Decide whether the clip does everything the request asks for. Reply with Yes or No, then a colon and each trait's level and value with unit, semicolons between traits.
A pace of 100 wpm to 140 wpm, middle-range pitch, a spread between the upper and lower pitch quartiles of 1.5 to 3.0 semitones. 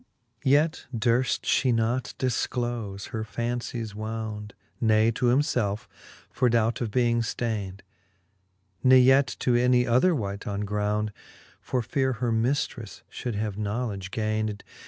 No: slow, 135 wpm; low, 115 Hz; average, 2.7 semitones